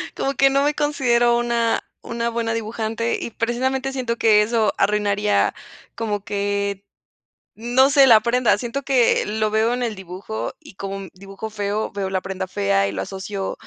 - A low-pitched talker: No, high, 220 Hz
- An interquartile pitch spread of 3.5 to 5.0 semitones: No, average, 3.1 semitones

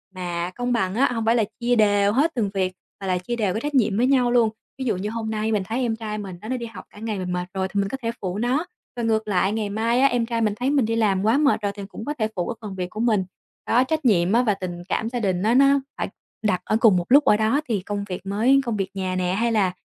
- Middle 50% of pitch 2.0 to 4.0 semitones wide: Yes, average, 3.6 semitones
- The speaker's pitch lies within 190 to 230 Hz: Yes, high, 220 Hz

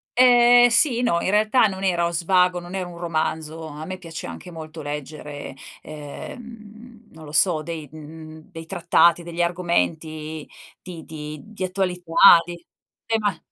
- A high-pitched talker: No, medium, 170 Hz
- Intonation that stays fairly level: No, average, 3.6 semitones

